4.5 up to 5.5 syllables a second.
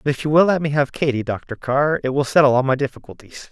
No: 6.2 syllables/s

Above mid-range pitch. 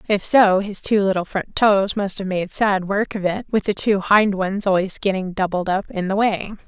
Yes: high, 195 Hz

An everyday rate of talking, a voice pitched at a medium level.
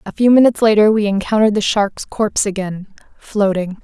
No: average, 170 wpm; high, 205 Hz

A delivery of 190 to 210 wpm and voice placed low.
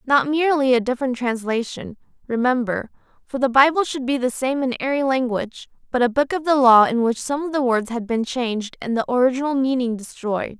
No: fast, 205 wpm; very high, 255 Hz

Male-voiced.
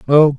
Yes: male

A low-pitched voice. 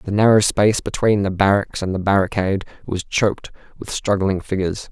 Yes: low, 100 Hz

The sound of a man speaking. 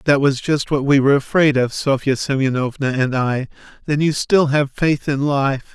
Yes: male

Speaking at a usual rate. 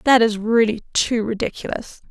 Yes: average, 145 wpm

